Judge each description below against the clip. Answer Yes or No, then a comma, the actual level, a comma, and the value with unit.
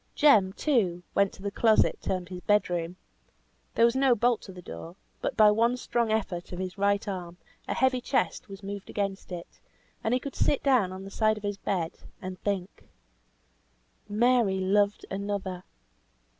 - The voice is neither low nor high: No, high, 200 Hz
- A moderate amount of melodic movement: Yes, average, 3.4 semitones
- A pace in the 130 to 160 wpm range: No, average, 180 wpm